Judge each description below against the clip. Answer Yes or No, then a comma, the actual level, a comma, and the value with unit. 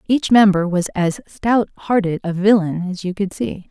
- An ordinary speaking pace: Yes, average, 195 wpm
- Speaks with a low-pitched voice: No, high, 195 Hz